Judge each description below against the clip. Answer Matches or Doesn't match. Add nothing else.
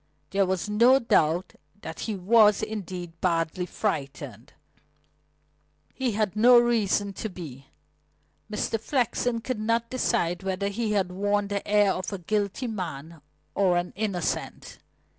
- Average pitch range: Matches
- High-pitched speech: Matches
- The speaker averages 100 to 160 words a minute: Matches